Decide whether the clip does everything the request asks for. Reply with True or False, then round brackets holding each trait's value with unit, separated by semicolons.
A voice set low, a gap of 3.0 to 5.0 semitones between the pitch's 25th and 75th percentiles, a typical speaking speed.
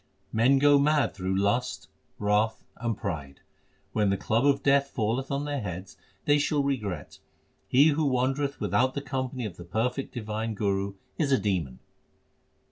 False (120 Hz; 5.4 semitones; 160 wpm)